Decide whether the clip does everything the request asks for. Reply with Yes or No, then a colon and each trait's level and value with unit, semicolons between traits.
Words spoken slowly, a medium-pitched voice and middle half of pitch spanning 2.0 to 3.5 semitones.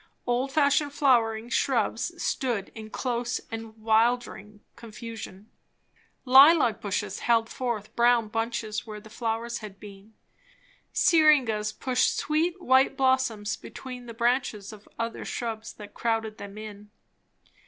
No: slow, 120 wpm; high, 230 Hz; average, 2.9 semitones